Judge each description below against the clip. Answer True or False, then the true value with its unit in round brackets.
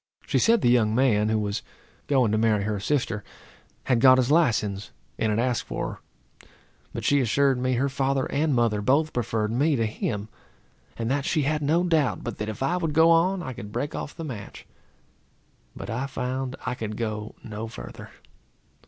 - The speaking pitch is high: False (125 Hz)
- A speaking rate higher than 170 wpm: True (195 wpm)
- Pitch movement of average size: True (4.6 semitones)